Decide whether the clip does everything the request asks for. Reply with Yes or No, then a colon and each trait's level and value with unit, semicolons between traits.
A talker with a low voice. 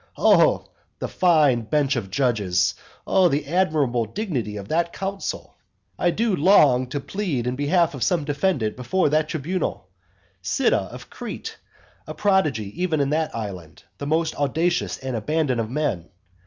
No: medium, 145 Hz